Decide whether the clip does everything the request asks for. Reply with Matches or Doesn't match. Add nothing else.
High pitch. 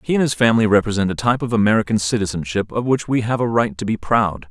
Doesn't match